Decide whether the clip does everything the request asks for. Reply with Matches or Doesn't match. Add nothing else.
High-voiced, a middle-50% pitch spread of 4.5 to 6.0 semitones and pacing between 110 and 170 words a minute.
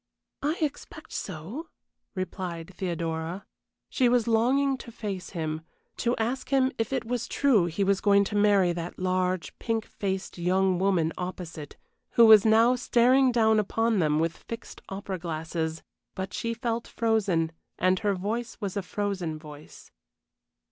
Matches